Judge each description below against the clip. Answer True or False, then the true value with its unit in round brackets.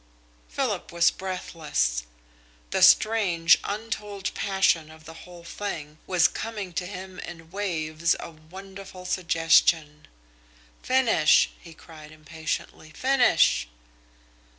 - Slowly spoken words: True (105 wpm)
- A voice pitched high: False (170 Hz)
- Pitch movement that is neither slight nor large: True (3.5 semitones)